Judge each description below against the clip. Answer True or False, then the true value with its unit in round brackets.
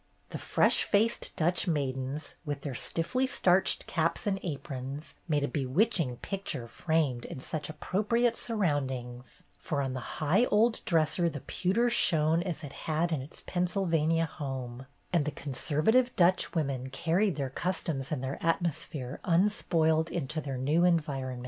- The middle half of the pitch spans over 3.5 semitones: True (4.6 semitones)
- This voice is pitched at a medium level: True (160 Hz)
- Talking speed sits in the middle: True (150 wpm)